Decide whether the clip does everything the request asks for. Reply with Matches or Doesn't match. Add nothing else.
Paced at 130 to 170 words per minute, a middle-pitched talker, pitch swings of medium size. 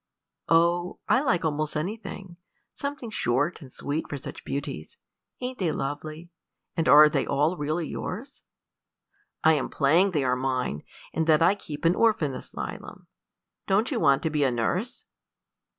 Matches